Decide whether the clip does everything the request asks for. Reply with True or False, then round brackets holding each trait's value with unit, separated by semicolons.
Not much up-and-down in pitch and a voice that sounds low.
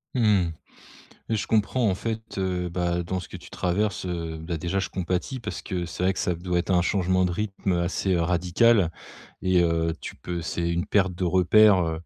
True (2.2 semitones; 90 Hz)